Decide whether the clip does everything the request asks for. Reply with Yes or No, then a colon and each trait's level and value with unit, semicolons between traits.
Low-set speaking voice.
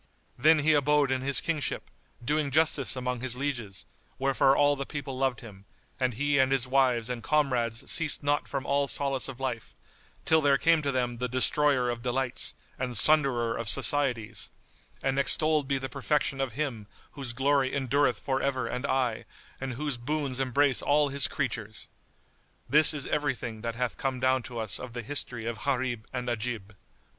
Yes: low, 130 Hz